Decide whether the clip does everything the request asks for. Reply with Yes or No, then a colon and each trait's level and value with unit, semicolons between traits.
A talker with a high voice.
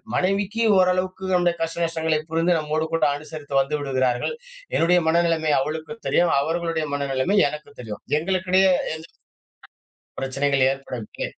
No: medium, 160 Hz